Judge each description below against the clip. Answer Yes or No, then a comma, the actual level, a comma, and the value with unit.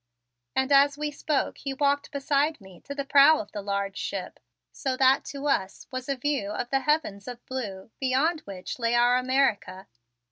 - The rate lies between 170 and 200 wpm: Yes, average, 185 wpm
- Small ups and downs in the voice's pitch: No, average, 5.1 semitones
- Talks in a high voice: Yes, very high, 265 Hz